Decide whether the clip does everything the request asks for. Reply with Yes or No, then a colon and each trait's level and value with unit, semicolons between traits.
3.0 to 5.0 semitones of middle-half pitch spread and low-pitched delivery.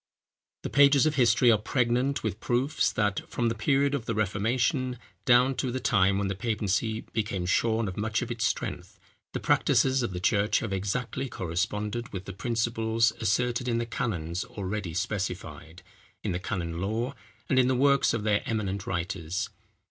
Yes: average, 4.0 semitones; low, 110 Hz